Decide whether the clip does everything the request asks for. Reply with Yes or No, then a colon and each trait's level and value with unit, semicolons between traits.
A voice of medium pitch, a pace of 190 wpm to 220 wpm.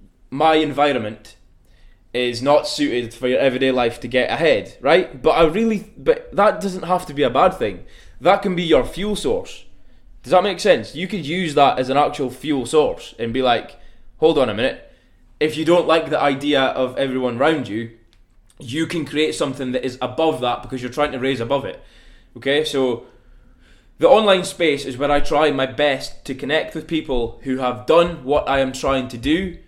Yes: medium, 145 Hz; average, 200 wpm